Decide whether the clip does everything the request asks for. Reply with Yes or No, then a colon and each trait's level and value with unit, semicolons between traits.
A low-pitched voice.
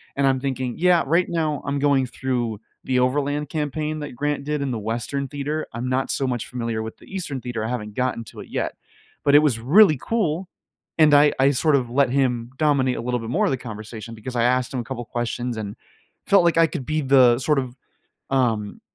Yes: low, 130 Hz